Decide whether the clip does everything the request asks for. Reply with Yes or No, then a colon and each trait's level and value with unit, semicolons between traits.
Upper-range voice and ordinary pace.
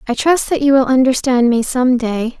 No: very high, 255 Hz; fast, 225 wpm